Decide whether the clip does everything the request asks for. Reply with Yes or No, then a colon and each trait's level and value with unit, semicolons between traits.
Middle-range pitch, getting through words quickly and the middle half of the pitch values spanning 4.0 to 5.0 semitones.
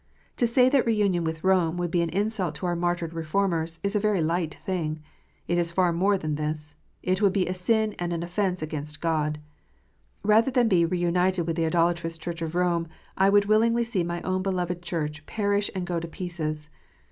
No: medium, 175 Hz; fast, 210 wpm; average, 3.0 semitones